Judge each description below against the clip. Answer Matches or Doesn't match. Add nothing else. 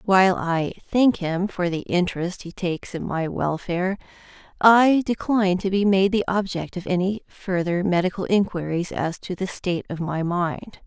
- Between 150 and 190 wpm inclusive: Matches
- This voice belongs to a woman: Matches